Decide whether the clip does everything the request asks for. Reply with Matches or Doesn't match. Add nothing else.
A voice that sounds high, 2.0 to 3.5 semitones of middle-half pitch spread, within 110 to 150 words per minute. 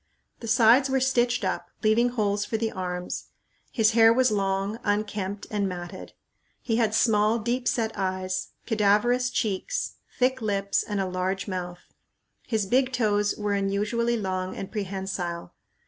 Matches